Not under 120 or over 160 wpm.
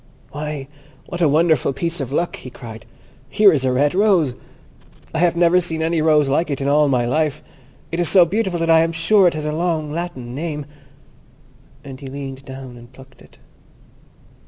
No: average, 195 wpm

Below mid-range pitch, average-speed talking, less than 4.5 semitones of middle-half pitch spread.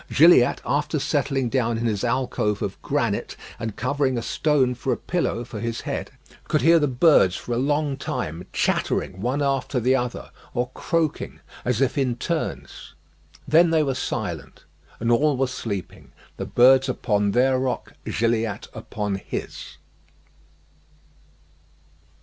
Yes: low, 125 Hz; average, 145 wpm; average, 3.4 semitones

